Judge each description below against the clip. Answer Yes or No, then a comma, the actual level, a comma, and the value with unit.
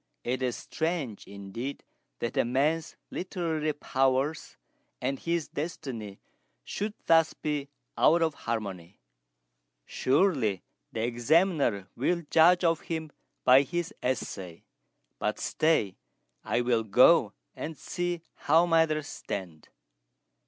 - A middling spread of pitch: No, wide, 5.8 semitones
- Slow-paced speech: Yes, slow, 110 wpm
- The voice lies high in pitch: No, medium, 145 Hz